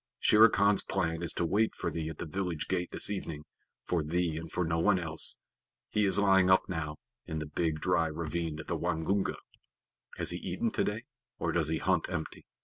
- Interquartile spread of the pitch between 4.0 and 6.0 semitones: No, average, 2.8 semitones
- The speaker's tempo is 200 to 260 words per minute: Yes, fast, 205 wpm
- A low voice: Yes, very low, 85 Hz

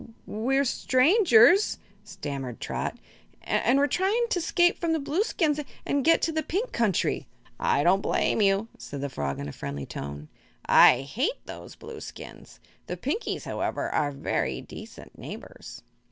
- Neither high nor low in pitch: No, very high, 255 Hz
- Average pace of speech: Yes, average, 155 wpm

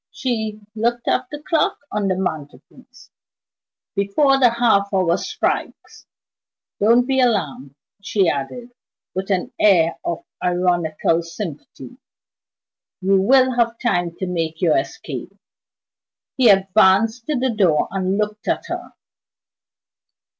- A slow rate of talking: Yes, slow, 120 wpm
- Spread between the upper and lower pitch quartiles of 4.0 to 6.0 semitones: Yes, average, 5.2 semitones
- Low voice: No, high, 200 Hz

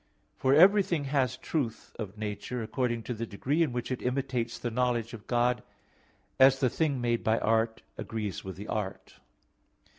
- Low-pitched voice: Yes, low, 120 Hz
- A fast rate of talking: No, average, 170 wpm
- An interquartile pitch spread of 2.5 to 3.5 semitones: Yes, average, 3.0 semitones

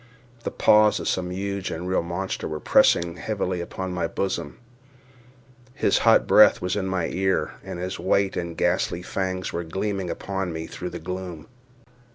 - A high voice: No, very low, 95 Hz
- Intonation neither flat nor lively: No, narrow, 2.3 semitones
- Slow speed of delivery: No, average, 160 wpm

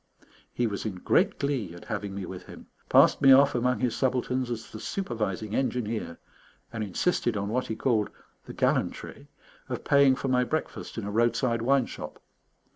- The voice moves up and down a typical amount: Yes, average, 3.5 semitones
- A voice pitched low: Yes, low, 120 Hz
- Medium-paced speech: Yes, average, 180 wpm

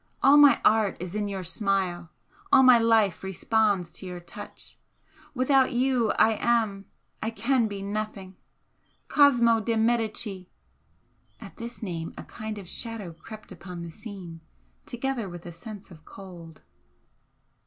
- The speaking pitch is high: Yes, high, 210 Hz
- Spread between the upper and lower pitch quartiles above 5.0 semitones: No, average, 4.1 semitones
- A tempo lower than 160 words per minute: Yes, average, 145 wpm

